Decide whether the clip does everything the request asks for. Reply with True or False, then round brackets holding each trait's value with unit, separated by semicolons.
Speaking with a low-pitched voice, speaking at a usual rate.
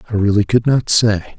False (105 Hz; 215 wpm)